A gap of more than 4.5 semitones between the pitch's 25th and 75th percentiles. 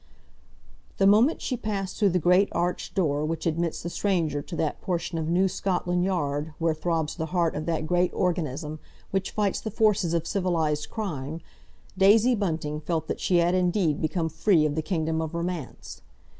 No: average, 3.3 semitones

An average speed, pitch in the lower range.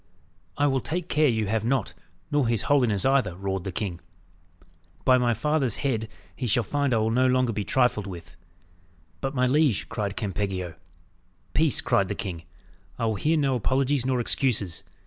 Yes: average, 175 wpm; low, 120 Hz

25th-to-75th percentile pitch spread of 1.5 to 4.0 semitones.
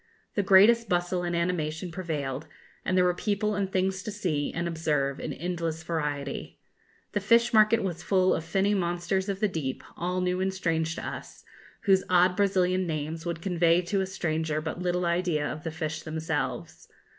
Yes: average, 2.8 semitones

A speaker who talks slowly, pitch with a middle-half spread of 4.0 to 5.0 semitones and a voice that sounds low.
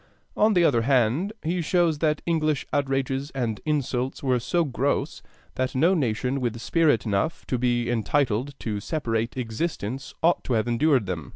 No: average, 165 wpm; average, 4.6 semitones; low, 130 Hz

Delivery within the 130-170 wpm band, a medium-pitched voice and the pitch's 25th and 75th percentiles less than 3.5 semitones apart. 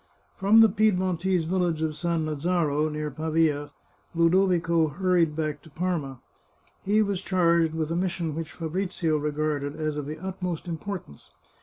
Yes: average, 145 wpm; medium, 165 Hz; average, 3.1 semitones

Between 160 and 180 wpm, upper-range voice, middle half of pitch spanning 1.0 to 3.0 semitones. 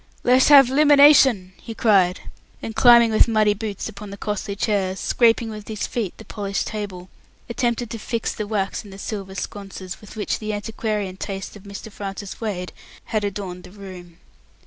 Yes: average, 175 wpm; high, 210 Hz; narrow, 2.5 semitones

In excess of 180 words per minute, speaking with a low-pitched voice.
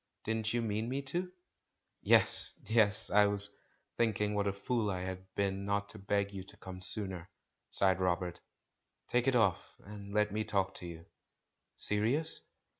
No: average, 170 wpm; low, 100 Hz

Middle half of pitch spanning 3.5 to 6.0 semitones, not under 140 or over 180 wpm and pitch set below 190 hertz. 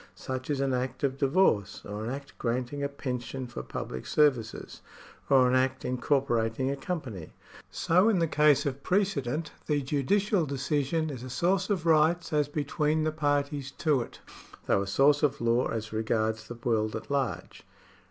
Yes: average, 3.9 semitones; average, 175 wpm; medium, 140 Hz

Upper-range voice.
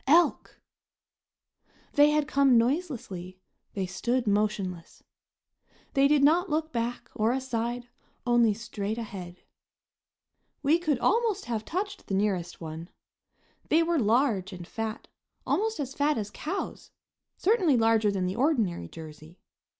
Yes: high, 235 Hz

